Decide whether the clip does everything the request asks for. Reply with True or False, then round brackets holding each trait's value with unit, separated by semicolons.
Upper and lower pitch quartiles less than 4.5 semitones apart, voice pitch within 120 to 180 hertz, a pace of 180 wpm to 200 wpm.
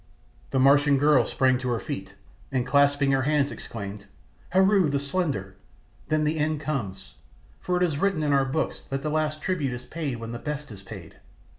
True (3.7 semitones; 140 Hz; 190 wpm)